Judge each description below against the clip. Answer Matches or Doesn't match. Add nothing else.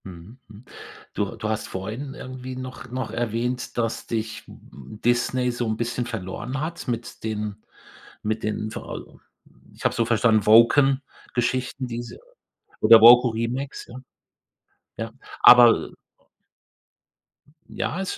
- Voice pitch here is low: Matches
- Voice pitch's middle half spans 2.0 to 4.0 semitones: Matches